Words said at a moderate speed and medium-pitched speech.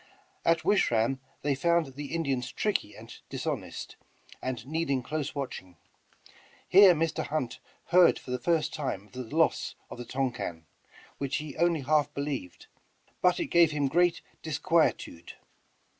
Yes: average, 145 wpm; medium, 145 Hz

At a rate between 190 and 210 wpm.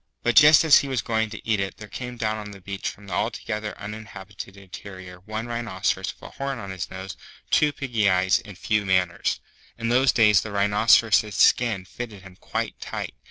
Yes: average, 200 wpm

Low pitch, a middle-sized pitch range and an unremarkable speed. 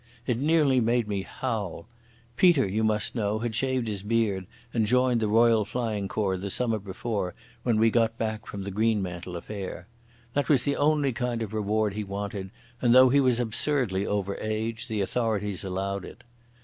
Yes: low, 110 Hz; average, 3.3 semitones; average, 180 wpm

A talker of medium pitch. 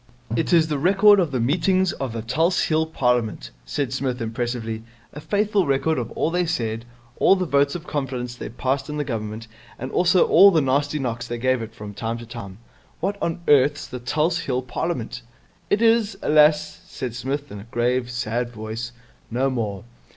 No: low, 130 Hz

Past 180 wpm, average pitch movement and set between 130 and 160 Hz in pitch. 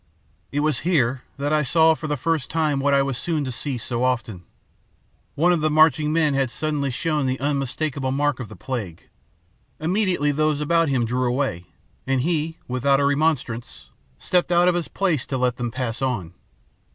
Yes: average, 190 wpm; average, 3.5 semitones; medium, 140 Hz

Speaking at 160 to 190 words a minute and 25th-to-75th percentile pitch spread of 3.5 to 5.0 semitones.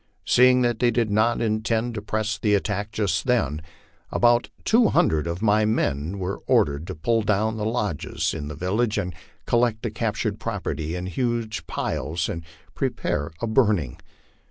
Yes: average, 165 wpm; average, 4.5 semitones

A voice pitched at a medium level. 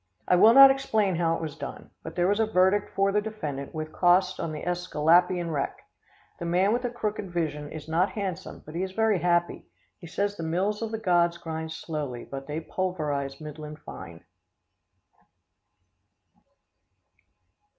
Yes: medium, 175 Hz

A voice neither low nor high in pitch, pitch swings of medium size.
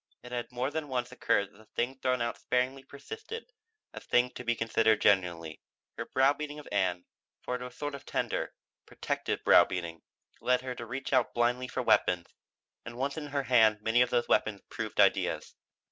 No: low, 125 Hz; average, 3.4 semitones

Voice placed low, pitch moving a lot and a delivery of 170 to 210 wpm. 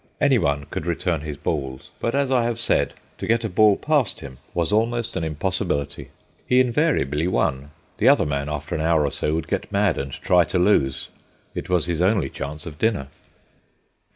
Yes: very low, 85 Hz; wide, 7.4 semitones; average, 190 wpm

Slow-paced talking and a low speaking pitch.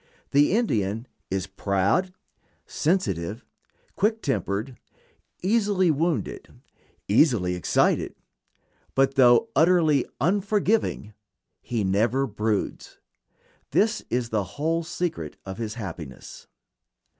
Yes: slow, 90 wpm; low, 130 Hz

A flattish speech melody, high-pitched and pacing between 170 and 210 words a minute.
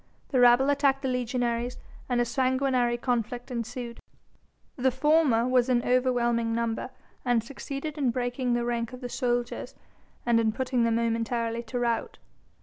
No: narrow, 1.6 semitones; high, 245 Hz; average, 150 wpm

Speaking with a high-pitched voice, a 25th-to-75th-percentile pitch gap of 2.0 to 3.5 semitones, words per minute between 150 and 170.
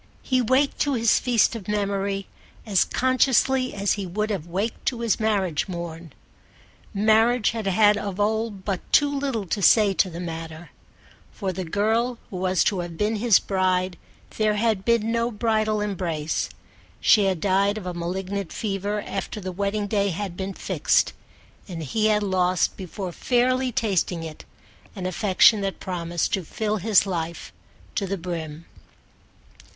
Yes: high, 200 Hz; average, 3.1 semitones; average, 160 wpm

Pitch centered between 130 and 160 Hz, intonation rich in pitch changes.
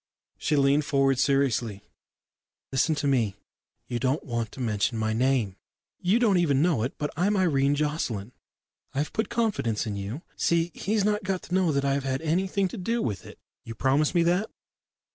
Yes: medium, 140 Hz; wide, 6.3 semitones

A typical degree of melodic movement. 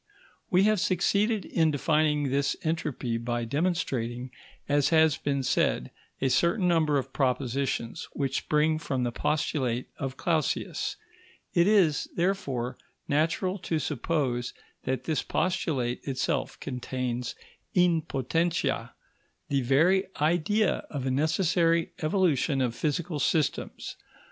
Yes: average, 4.4 semitones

